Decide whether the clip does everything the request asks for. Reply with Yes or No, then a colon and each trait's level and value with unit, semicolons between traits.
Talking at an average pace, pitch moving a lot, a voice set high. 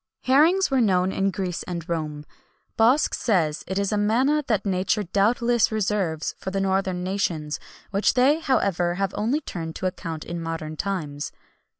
No: average, 165 wpm; average, 4.5 semitones; high, 195 Hz